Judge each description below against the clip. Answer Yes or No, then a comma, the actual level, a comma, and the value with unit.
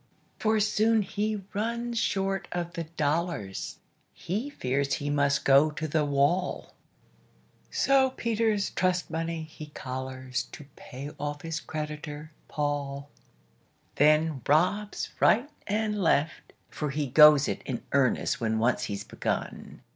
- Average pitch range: No, wide, 6.0 semitones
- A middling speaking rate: No, slow, 130 wpm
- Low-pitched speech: No, medium, 155 Hz